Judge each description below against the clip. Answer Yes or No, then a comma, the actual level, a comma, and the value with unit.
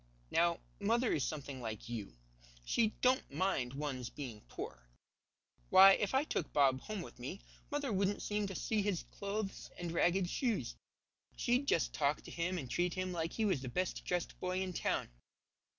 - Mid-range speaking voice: Yes, medium, 180 Hz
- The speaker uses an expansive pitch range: Yes, wide, 6.4 semitones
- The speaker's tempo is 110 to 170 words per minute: No, average, 180 wpm